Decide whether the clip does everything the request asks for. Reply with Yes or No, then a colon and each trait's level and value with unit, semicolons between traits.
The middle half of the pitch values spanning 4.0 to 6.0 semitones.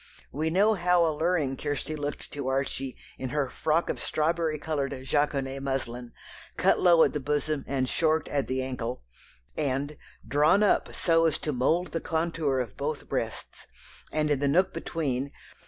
No: average, 3.1 semitones